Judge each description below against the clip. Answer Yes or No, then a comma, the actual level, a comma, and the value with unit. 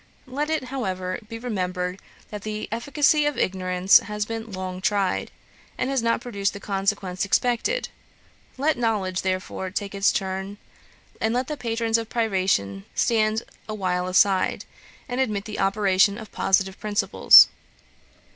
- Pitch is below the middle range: No, high, 205 Hz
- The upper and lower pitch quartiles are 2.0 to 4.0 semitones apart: Yes, average, 3.5 semitones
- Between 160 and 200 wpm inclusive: No, average, 140 wpm